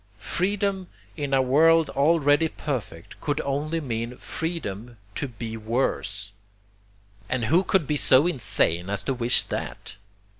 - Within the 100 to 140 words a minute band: Yes, slow, 135 wpm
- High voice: No, low, 135 Hz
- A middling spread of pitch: No, wide, 5.9 semitones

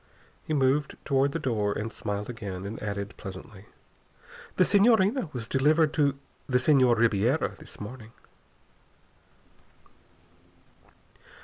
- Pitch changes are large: Yes, wide, 6.1 semitones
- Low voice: Yes, low, 125 Hz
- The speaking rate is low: Yes, slow, 110 wpm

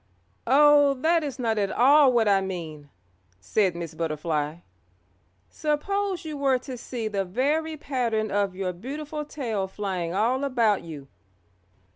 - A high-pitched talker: Yes, high, 230 Hz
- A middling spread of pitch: No, wide, 7.3 semitones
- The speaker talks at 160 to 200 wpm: No, average, 140 wpm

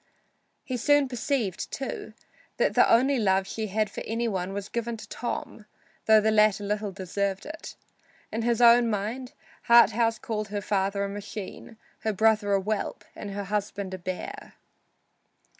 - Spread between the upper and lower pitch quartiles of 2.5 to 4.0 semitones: Yes, average, 2.8 semitones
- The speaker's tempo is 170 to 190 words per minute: No, average, 160 wpm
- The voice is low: No, high, 215 Hz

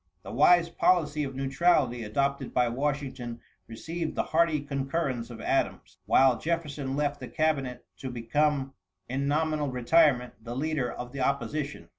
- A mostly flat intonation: No, average, 3.3 semitones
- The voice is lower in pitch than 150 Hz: Yes, medium, 140 Hz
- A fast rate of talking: No, average, 145 wpm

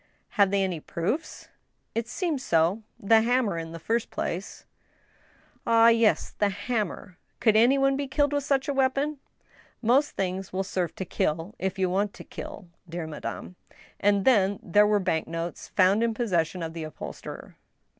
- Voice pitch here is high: Yes, high, 205 Hz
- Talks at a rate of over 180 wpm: Yes, average, 195 wpm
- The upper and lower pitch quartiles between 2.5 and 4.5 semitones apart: No, average, 4.9 semitones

